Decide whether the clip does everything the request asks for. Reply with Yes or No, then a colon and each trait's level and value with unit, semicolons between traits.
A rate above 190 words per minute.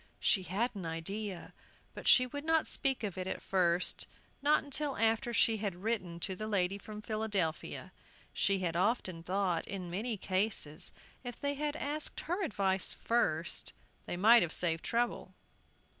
No: average, 160 wpm